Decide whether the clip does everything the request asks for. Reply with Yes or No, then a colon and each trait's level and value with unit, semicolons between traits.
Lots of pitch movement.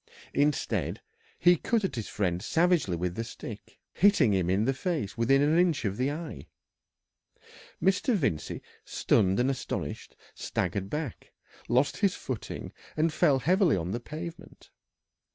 Yes: wide, 8.6 semitones